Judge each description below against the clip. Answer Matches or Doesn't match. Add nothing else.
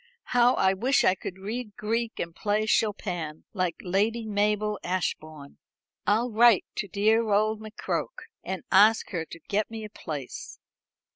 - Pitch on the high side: Matches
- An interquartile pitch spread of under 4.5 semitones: Matches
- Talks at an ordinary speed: Matches